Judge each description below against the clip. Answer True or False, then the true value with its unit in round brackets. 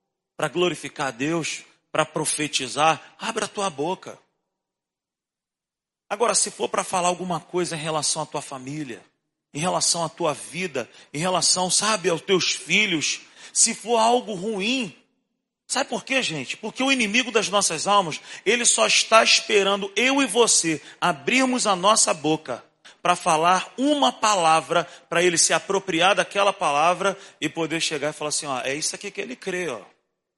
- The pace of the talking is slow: False (160 wpm)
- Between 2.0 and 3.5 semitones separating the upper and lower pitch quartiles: False (5.0 semitones)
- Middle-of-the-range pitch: True (180 Hz)